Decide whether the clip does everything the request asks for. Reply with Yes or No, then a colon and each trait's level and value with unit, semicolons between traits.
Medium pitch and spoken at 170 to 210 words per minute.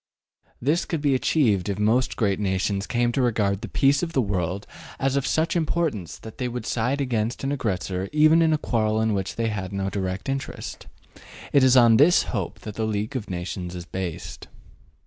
No: low, 110 Hz; average, 200 wpm